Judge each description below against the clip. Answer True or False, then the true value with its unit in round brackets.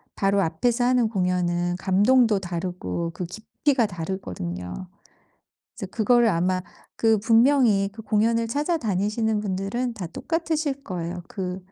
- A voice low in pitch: False (200 Hz)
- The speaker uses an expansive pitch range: False (4.5 semitones)